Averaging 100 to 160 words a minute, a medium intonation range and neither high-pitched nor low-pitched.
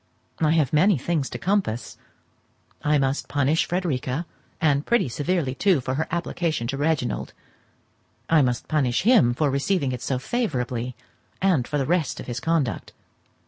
Yes: average, 155 wpm; average, 4.7 semitones; medium, 145 Hz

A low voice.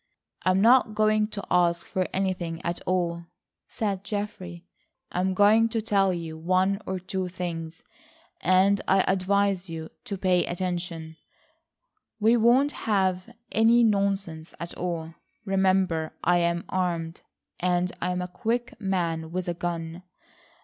No: medium, 185 Hz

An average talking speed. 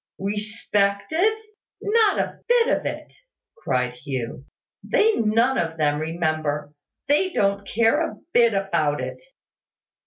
No: slow, 120 wpm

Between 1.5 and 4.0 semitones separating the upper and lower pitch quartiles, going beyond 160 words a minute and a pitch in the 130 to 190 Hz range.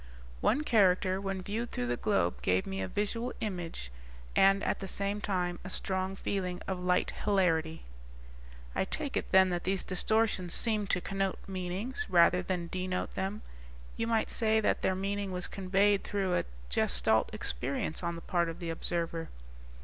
Yes: narrow, 2.5 semitones; average, 170 wpm; medium, 185 Hz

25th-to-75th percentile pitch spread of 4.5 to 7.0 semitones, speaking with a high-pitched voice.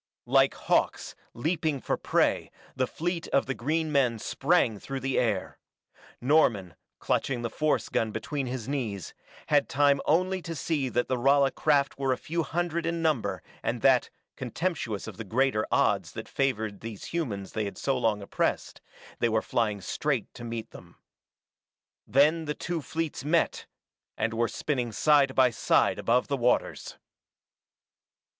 No: average, 5.1 semitones; low, 135 Hz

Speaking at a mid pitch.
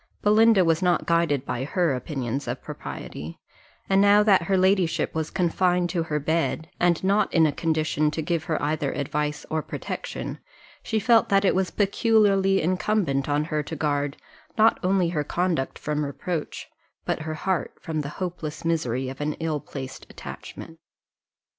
Yes: medium, 165 Hz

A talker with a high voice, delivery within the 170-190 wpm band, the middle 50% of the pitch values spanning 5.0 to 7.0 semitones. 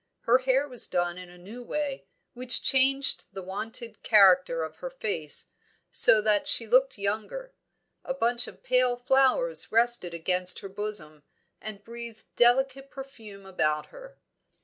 No: high, 230 Hz; average, 150 wpm; wide, 5.5 semitones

